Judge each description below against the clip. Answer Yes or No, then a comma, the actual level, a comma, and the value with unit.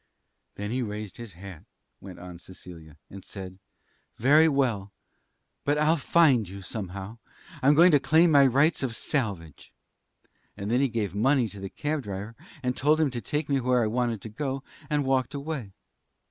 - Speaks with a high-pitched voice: No, low, 120 Hz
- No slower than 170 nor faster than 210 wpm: Yes, average, 175 wpm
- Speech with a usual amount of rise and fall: No, wide, 6.1 semitones